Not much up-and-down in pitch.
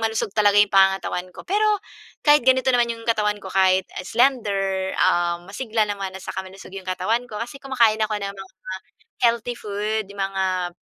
No: average, 3.3 semitones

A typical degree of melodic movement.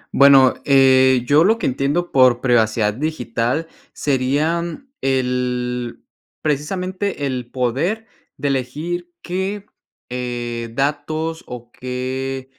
Yes: average, 4.2 semitones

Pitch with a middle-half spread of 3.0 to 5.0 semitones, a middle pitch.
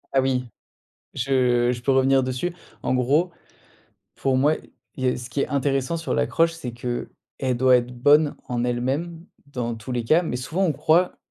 No: average, 3.4 semitones; low, 130 Hz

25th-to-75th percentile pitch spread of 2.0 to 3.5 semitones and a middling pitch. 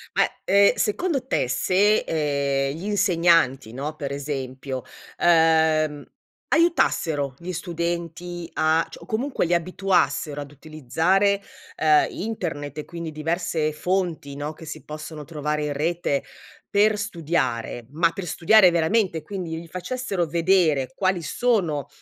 No: average, 3.9 semitones; medium, 165 Hz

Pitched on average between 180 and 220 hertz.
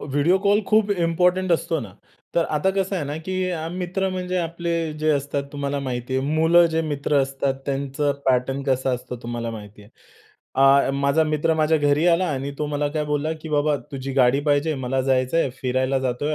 No: medium, 145 Hz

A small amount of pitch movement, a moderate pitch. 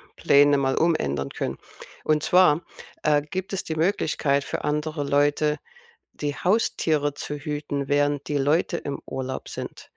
Yes: narrow, 1.8 semitones; medium, 145 Hz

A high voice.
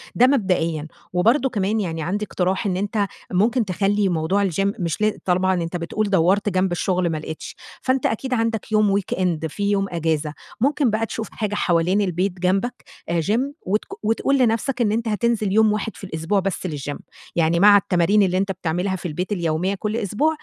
Yes: high, 195 Hz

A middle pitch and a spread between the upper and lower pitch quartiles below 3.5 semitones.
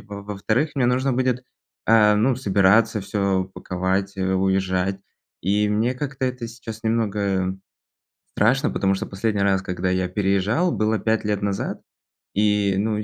No: low, 105 Hz; average, 2.9 semitones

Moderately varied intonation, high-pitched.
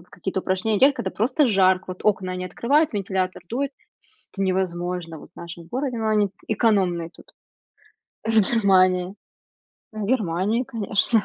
Yes: average, 3.4 semitones; high, 195 Hz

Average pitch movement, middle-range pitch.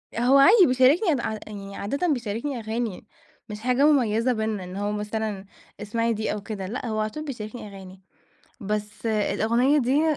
No: average, 3.6 semitones; high, 220 Hz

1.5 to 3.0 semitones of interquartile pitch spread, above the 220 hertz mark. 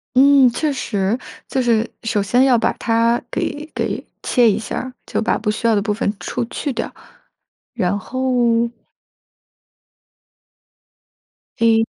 Yes: average, 2.7 semitones; high, 230 Hz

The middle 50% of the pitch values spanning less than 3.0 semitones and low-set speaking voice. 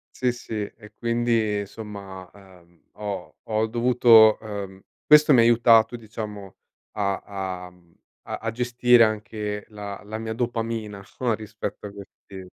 Yes: narrow, 2.6 semitones; low, 110 Hz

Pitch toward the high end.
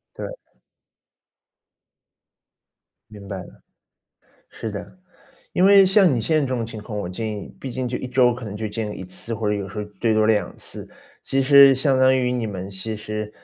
No: low, 115 Hz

